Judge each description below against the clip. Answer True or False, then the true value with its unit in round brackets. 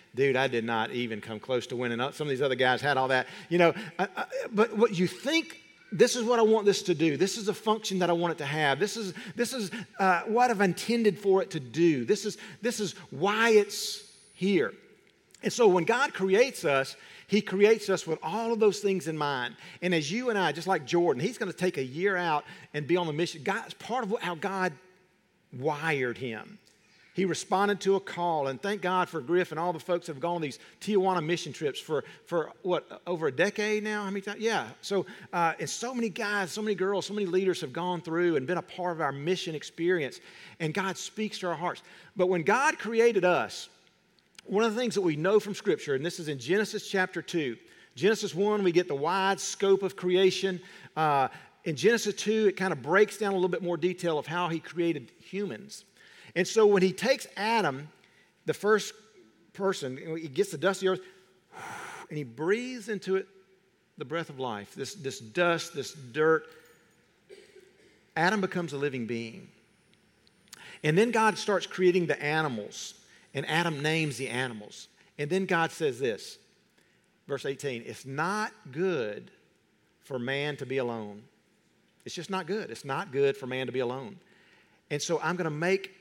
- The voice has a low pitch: False (185 Hz)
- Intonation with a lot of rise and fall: False (4.4 semitones)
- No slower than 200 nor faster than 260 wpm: True (205 wpm)